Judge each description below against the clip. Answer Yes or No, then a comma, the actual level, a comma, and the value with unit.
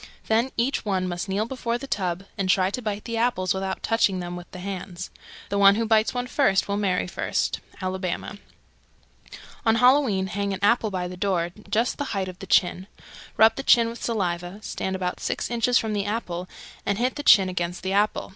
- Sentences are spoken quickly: Yes, fast, 210 wpm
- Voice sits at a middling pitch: No, high, 200 Hz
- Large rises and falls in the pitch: No, average, 3.6 semitones